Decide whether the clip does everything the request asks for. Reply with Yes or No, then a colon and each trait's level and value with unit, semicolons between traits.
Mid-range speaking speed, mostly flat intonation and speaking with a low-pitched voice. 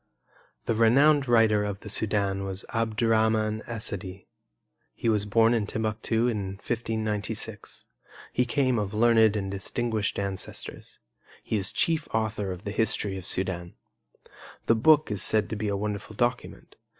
Yes: average, 145 wpm; narrow, 2.2 semitones; low, 110 Hz